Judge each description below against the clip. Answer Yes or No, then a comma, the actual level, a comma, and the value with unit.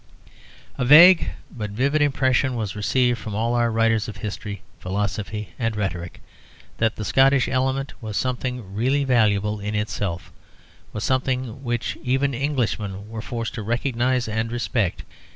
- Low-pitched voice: Yes, low, 115 Hz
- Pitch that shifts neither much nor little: Yes, average, 3.5 semitones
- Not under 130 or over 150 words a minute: Yes, average, 145 wpm